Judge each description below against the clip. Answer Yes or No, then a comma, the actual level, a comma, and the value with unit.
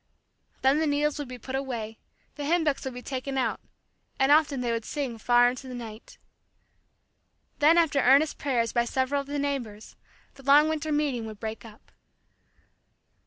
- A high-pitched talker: Yes, very high, 270 Hz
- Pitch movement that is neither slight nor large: Yes, average, 3.2 semitones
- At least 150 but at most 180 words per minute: Yes, average, 175 wpm